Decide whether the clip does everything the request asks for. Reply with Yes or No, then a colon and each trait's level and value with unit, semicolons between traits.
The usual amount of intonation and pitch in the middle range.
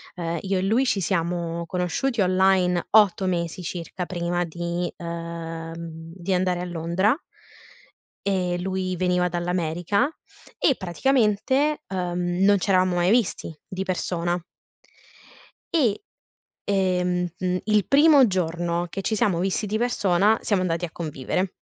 No: narrow, 2.3 semitones; medium, 180 Hz